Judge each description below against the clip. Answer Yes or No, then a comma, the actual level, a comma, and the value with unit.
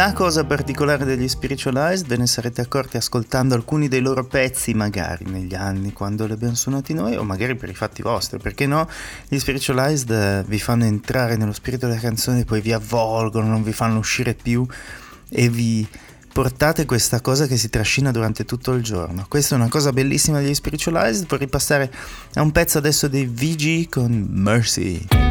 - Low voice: Yes, low, 125 Hz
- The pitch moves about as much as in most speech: Yes, average, 4.0 semitones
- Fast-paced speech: Yes, fast, 180 wpm